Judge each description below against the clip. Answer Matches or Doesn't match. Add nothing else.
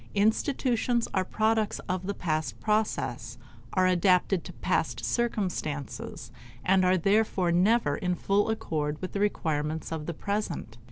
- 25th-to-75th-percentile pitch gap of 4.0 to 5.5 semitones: Matches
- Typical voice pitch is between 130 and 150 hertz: Doesn't match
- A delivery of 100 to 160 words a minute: Matches